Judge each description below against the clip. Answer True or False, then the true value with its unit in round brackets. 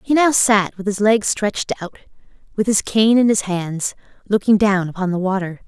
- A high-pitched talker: True (205 Hz)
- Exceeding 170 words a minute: True (200 wpm)